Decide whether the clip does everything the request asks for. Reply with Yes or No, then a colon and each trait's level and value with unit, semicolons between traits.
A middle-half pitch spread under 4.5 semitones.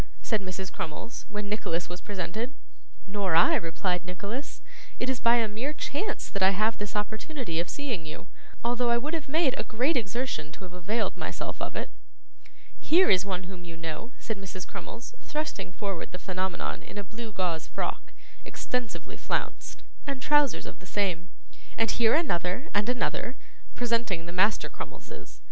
No: average, 5.2 semitones